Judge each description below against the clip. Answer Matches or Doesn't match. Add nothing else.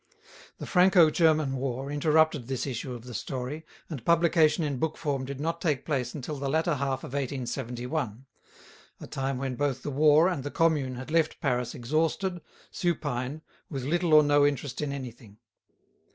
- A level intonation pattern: Doesn't match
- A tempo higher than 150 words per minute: Matches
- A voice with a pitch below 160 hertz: Matches